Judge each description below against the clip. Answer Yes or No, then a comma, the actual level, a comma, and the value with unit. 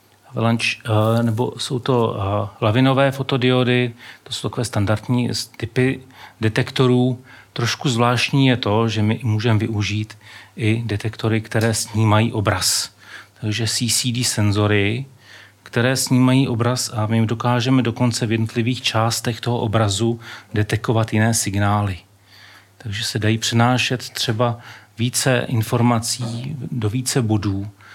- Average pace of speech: No, slow, 110 wpm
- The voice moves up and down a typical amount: No, narrow, 2.3 semitones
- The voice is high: No, low, 115 Hz